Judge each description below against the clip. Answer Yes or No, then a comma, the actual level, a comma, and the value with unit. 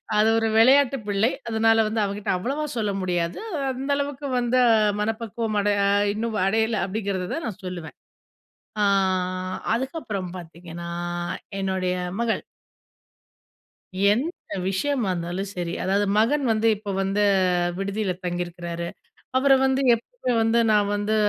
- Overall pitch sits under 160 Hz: No, high, 210 Hz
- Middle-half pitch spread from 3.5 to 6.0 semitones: Yes, average, 3.9 semitones